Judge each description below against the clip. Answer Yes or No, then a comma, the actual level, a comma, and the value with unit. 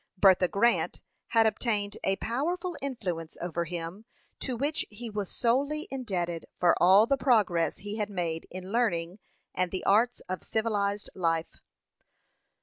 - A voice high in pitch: Yes, high, 205 Hz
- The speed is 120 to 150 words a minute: Yes, average, 145 wpm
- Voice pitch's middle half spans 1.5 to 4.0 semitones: No, average, 5.0 semitones